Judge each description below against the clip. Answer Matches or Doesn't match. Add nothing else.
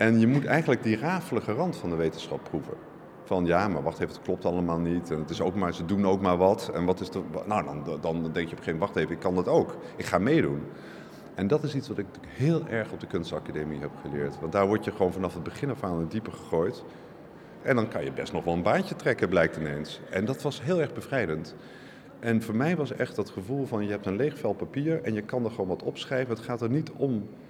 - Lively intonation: Matches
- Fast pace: Matches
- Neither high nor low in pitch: Doesn't match